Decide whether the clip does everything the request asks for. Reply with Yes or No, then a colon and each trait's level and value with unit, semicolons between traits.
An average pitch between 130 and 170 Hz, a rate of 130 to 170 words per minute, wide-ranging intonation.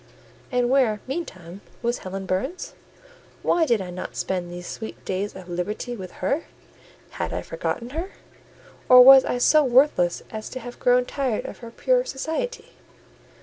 No: high, 240 Hz; average, 160 wpm; wide, 6.1 semitones